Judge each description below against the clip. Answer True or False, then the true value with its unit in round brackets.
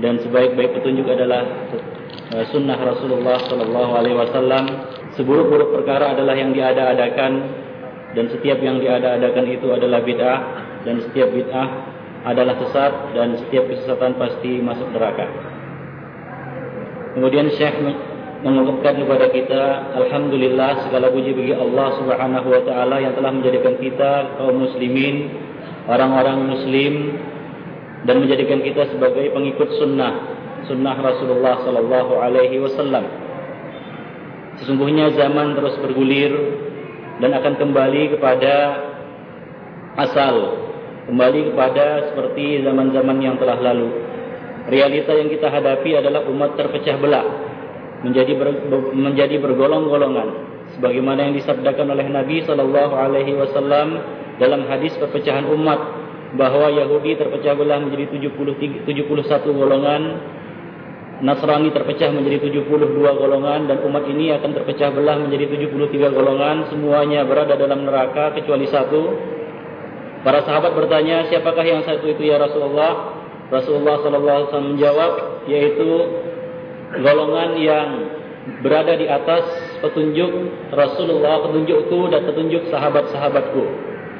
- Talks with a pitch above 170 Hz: False (140 Hz)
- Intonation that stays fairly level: True (2.2 semitones)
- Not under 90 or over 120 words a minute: True (115 wpm)